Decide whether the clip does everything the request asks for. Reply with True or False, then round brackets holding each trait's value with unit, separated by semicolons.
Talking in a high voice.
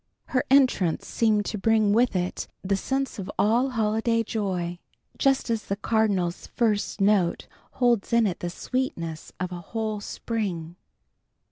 True (215 Hz)